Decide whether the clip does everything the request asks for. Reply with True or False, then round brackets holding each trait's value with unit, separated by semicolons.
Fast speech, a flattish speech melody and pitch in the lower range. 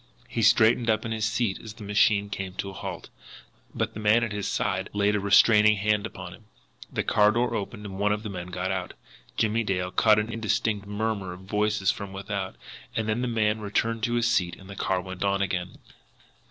True (215 wpm; 2.3 semitones; 105 Hz)